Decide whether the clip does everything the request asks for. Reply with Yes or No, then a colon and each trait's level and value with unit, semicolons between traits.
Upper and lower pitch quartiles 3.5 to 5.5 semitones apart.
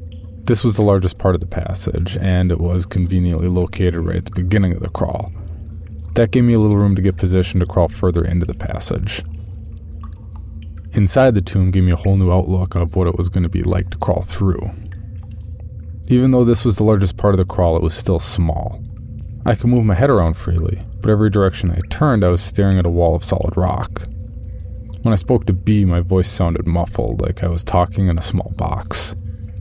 No: narrow, 2.4 semitones